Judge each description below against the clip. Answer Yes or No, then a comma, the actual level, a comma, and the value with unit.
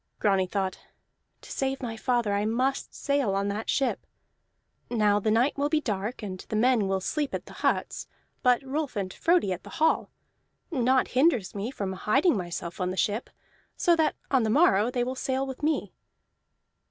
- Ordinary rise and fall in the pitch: Yes, average, 5.0 semitones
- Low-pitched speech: No, high, 235 Hz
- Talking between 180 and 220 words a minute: Yes, average, 185 wpm